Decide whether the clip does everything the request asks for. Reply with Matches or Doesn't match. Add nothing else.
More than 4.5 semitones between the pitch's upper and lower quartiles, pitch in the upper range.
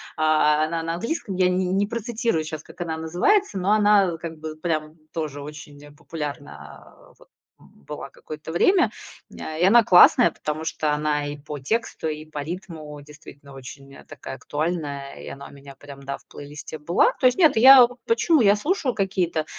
Doesn't match